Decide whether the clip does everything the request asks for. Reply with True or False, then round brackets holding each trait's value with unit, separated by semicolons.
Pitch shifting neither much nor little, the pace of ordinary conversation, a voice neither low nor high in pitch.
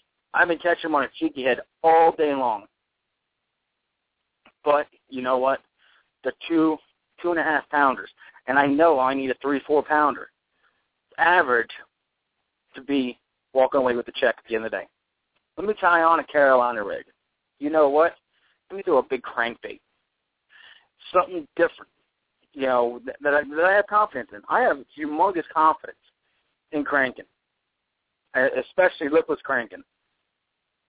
True (3.9 semitones; 155 wpm; 150 Hz)